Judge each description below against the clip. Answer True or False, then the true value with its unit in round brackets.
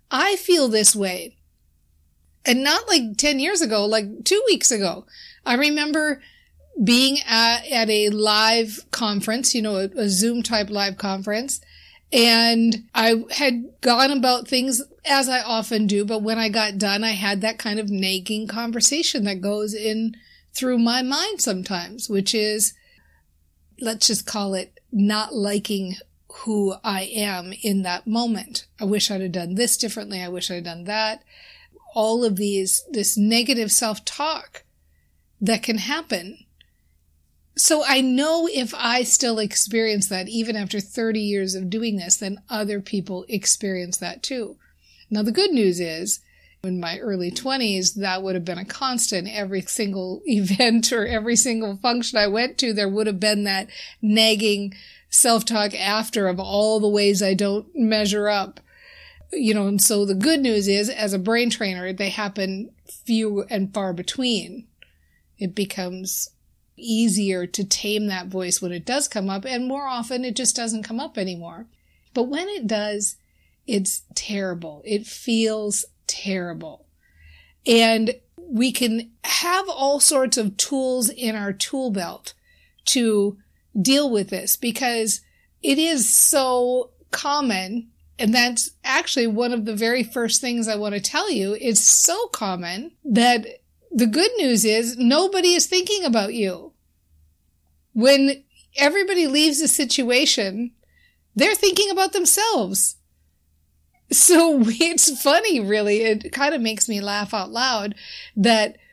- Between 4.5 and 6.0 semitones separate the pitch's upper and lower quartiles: False (3.9 semitones)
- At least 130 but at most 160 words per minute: True (155 wpm)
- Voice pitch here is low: False (220 Hz)